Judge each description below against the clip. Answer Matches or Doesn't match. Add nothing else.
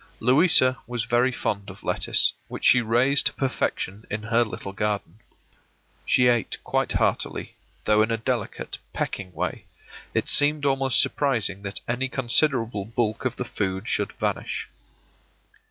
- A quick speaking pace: Doesn't match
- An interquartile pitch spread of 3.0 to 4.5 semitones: Matches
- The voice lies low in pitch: Matches